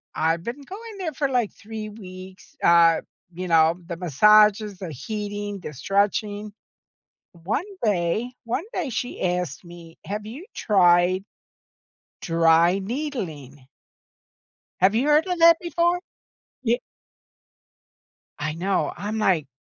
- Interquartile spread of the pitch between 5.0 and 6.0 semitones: Yes, wide, 5.4 semitones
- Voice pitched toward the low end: No, high, 200 Hz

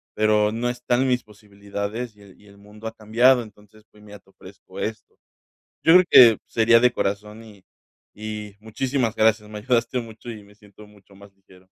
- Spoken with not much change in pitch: Yes, narrow, 2.1 semitones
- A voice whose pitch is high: No, low, 110 Hz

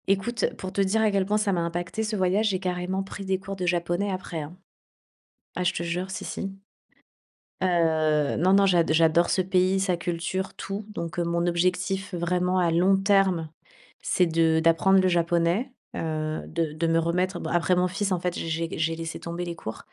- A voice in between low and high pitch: Yes, medium, 180 Hz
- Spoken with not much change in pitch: Yes, narrow, 2.3 semitones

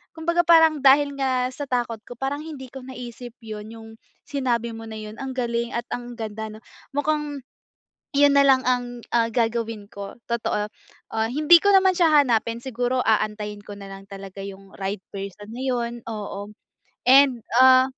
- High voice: Yes, high, 240 Hz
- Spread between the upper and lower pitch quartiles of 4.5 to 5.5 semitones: No, average, 3.8 semitones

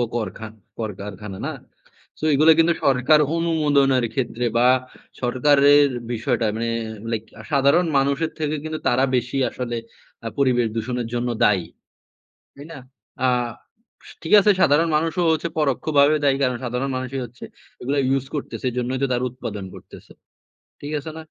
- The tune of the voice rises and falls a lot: No, average, 3.4 semitones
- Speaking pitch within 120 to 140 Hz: Yes, low, 135 Hz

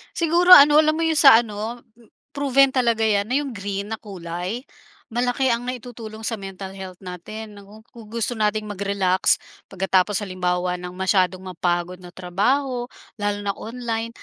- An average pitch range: Yes, average, 4.4 semitones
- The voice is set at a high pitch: Yes, high, 215 Hz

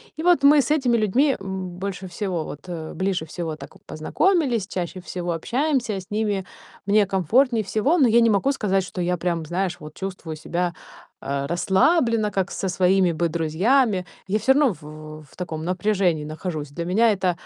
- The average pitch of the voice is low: No, high, 190 Hz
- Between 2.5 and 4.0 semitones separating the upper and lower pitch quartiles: No, average, 4.7 semitones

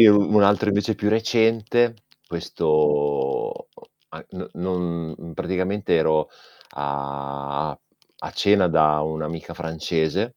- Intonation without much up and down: No, average, 5.2 semitones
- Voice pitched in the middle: No, very low, 85 Hz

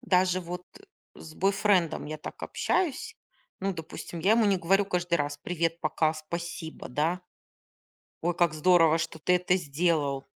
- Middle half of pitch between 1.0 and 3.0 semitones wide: Yes, narrow, 2.6 semitones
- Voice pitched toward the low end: No, medium, 175 Hz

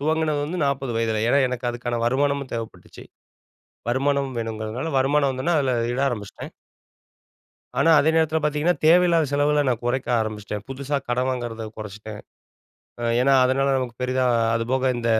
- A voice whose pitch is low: Yes, low, 130 Hz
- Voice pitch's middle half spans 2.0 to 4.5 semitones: Yes, average, 3.3 semitones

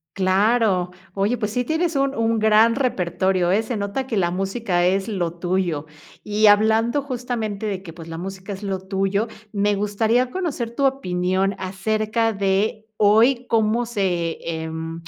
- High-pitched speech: Yes, high, 205 Hz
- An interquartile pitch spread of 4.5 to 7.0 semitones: No, average, 3.5 semitones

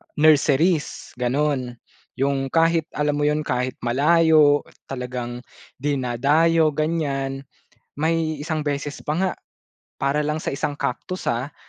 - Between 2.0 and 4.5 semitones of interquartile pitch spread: Yes, narrow, 2.5 semitones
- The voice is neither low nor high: Yes, medium, 145 Hz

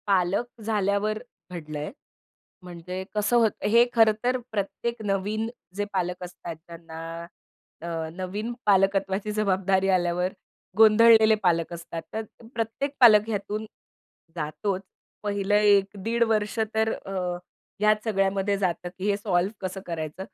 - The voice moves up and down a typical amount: Yes, average, 3.0 semitones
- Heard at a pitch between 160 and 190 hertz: No, high, 200 Hz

